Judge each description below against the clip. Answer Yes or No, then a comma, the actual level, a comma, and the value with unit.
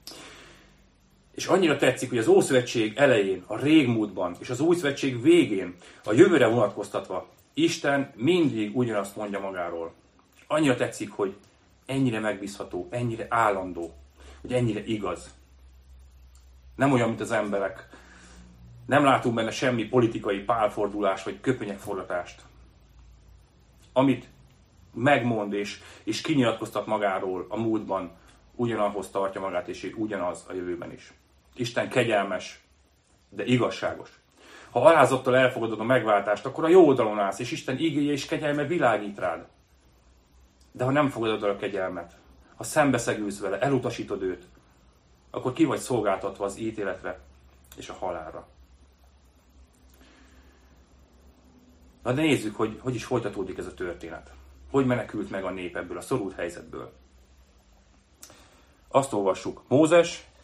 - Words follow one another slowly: No, average, 125 wpm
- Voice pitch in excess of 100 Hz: No, very low, 95 Hz